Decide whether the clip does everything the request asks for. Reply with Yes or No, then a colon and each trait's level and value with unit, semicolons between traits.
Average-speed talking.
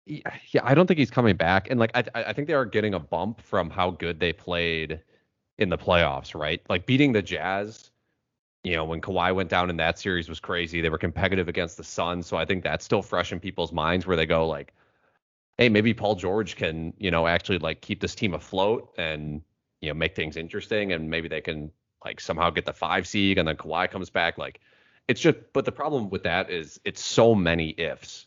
No: fast, 225 wpm